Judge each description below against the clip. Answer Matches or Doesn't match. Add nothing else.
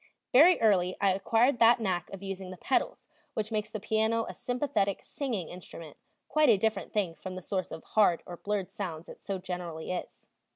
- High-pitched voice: Matches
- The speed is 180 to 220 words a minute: Matches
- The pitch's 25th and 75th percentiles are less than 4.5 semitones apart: Matches